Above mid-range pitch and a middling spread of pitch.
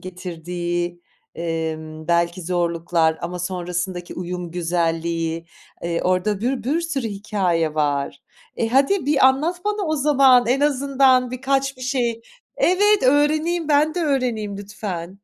No: high, 200 Hz; wide, 8.0 semitones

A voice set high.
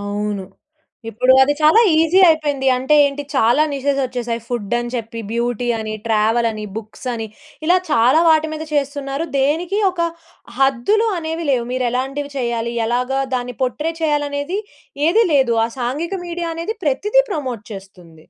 Yes: very high, 265 Hz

